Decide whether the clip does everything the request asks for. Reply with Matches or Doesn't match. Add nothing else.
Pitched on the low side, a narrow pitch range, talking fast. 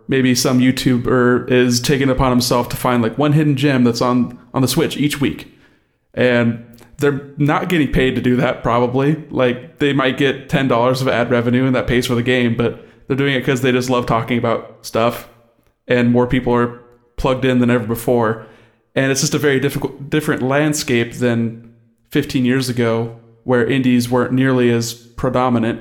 Doesn't match